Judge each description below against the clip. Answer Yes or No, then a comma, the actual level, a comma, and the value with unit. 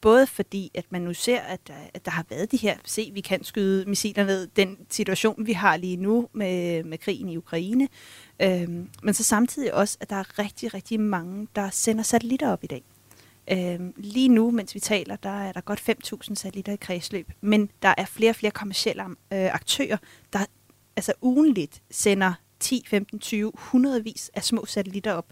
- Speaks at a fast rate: No, average, 200 wpm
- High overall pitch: Yes, high, 200 Hz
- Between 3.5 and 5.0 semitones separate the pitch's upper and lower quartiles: No, average, 3.1 semitones